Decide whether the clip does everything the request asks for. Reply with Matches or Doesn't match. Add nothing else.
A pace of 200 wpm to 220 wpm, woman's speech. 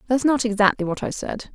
Doesn't match